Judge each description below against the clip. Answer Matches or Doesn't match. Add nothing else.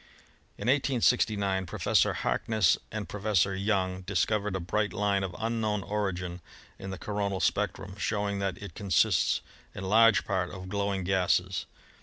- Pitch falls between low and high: Doesn't match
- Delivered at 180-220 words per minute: Doesn't match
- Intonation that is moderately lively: Doesn't match